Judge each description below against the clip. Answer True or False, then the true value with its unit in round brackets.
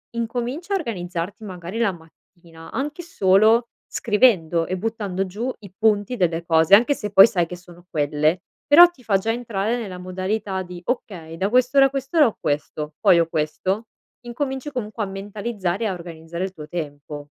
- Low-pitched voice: False (195 Hz)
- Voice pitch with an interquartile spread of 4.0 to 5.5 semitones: True (5.2 semitones)